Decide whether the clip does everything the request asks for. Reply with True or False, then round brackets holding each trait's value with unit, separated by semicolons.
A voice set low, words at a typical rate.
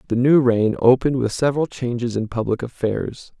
True (125 Hz; 175 wpm)